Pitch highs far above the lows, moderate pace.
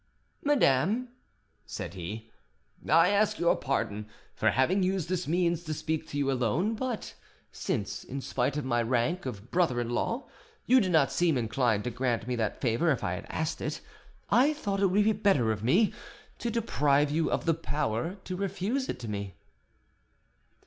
Yes: wide, 7.9 semitones; average, 175 wpm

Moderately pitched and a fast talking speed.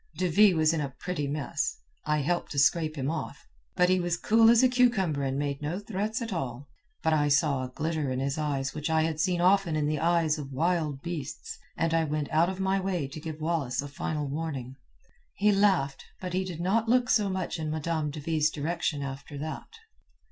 Yes: medium, 160 Hz; fast, 215 wpm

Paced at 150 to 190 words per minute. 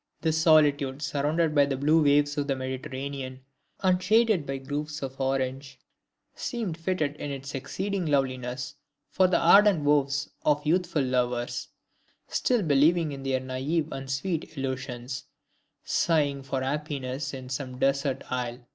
No: average, 140 wpm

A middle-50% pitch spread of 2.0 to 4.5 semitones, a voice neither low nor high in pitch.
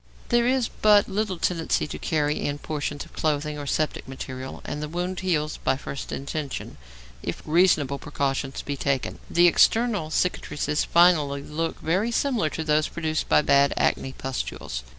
Yes: average, 4.0 semitones; medium, 155 Hz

